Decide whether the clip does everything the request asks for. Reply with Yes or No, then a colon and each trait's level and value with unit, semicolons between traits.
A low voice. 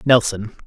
Yes: low, 110 Hz